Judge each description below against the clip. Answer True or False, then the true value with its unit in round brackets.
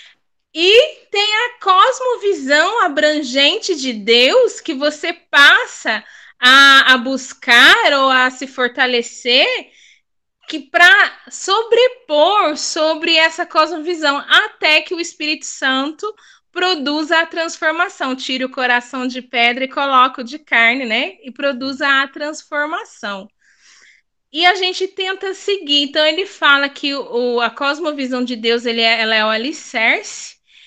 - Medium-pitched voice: False (300 Hz)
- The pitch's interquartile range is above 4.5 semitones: True (5.3 semitones)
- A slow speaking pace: False (130 wpm)